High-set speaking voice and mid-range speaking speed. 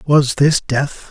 No: medium, 140 Hz; average, 165 wpm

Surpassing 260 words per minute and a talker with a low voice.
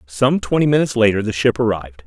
No: fast, 205 wpm; low, 115 Hz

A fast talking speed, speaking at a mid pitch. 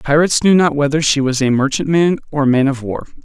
Yes: fast, 240 wpm; medium, 145 Hz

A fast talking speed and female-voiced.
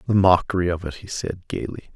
No: fast, 215 wpm; male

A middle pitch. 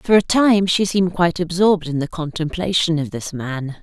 Yes: medium, 170 Hz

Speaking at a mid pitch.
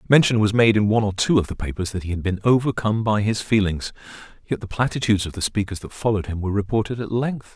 No: low, 105 Hz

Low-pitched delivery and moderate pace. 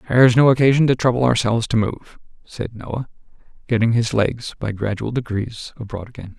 Yes: low, 115 Hz; average, 170 wpm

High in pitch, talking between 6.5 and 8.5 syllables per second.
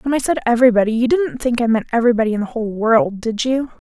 Yes: high, 240 Hz; 7.1 syllables/s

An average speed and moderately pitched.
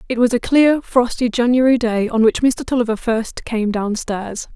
No: average, 185 wpm; high, 235 Hz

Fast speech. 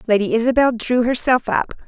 No: average, 160 wpm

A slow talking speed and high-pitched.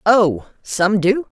Yes: slow, 130 wpm; high, 200 Hz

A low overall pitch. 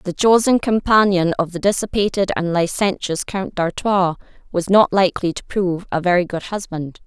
No: medium, 185 Hz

